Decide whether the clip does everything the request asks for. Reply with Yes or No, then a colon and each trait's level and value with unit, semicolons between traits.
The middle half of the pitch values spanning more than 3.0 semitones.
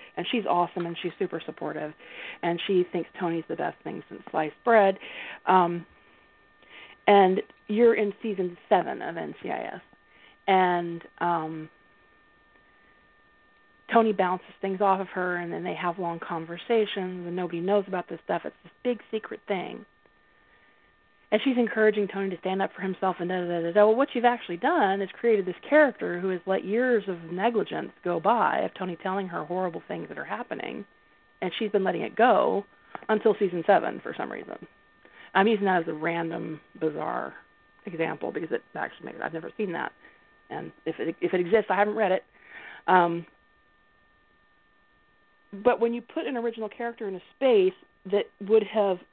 Yes: average, 3.7 semitones